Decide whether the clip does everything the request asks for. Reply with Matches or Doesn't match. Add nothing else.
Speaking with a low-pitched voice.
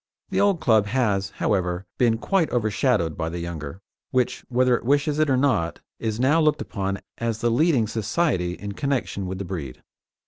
Matches